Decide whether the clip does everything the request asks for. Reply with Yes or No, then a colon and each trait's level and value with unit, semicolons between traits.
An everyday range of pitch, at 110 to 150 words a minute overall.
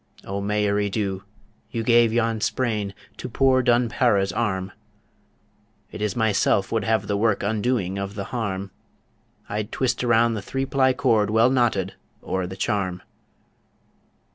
Yes: average, 3.2 semitones; average, 145 wpm